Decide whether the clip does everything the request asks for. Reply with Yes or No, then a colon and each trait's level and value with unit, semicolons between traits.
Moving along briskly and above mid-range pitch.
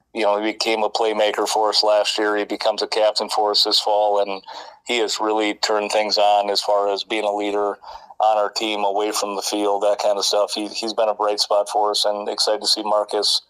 No: fast, 245 wpm; low, 105 Hz